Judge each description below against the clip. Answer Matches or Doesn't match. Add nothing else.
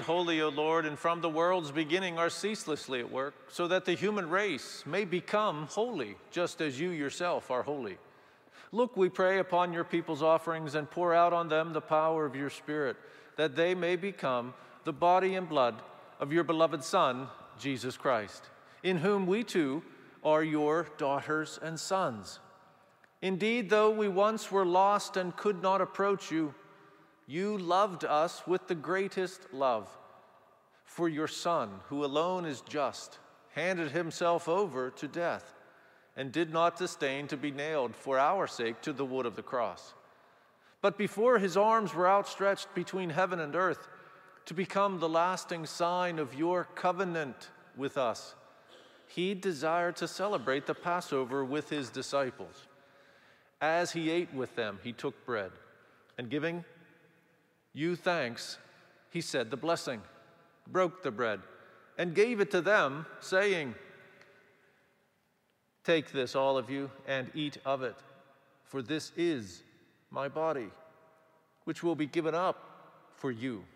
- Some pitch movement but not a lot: Matches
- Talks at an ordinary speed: Matches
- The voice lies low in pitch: Doesn't match